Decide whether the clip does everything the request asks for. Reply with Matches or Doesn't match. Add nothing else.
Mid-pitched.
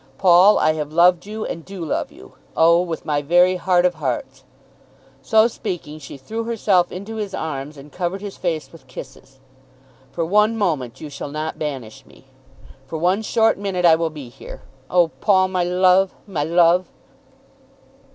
Matches